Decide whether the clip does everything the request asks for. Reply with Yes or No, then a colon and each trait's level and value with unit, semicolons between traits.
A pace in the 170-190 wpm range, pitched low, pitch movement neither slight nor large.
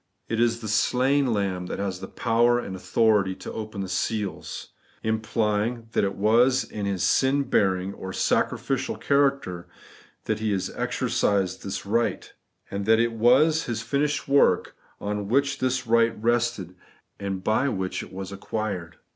No: average, 155 wpm; low, 110 Hz; average, 3.5 semitones